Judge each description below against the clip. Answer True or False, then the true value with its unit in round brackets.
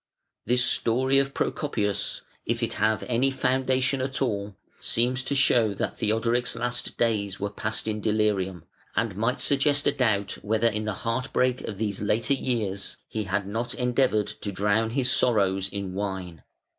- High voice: False (110 Hz)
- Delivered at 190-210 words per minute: False (170 wpm)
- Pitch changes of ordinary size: True (3.8 semitones)